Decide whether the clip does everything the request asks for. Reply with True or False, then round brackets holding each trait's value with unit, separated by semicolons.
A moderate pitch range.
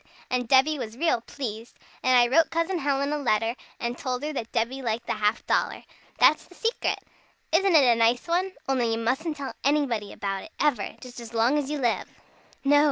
True (4.4 semitones)